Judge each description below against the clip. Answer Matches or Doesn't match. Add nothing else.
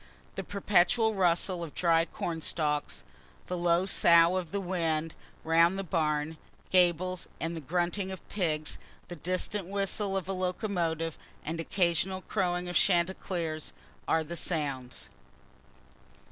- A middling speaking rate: Doesn't match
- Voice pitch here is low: Doesn't match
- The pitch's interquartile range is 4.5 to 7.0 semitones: Doesn't match